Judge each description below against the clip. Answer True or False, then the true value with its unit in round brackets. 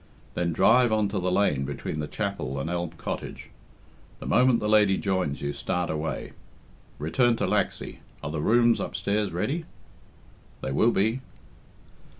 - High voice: False (95 Hz)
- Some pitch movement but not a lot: False (6.1 semitones)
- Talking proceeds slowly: False (155 wpm)